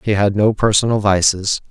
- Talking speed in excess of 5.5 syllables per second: No, 5.2 syllables/s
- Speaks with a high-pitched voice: No, low, 105 Hz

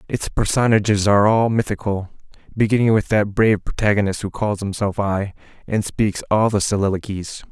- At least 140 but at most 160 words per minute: Yes, average, 150 wpm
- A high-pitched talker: No, low, 105 Hz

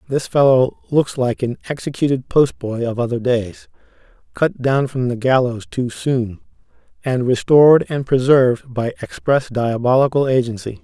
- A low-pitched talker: Yes, low, 125 Hz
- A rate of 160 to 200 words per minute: No, average, 140 wpm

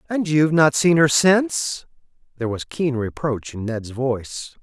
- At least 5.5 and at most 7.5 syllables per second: No, 4.7 syllables/s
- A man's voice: Yes, male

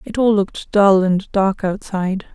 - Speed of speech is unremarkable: Yes, average, 180 wpm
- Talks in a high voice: Yes, high, 195 Hz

